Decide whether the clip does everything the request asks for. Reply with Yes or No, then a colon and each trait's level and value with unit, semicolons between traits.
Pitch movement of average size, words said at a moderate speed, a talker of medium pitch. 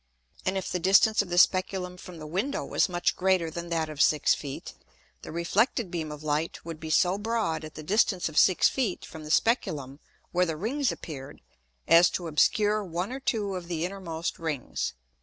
Yes: average, 3.6 semitones; average, 195 wpm; medium, 175 Hz